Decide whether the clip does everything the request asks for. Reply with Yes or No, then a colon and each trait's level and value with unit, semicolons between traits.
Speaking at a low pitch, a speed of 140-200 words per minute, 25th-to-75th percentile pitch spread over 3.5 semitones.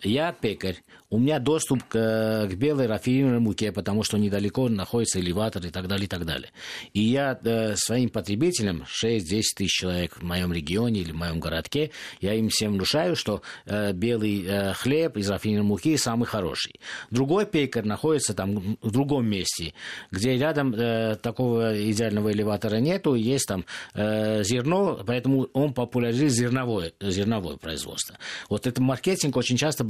Yes: low, 110 Hz; fast, 160 wpm; average, 4.0 semitones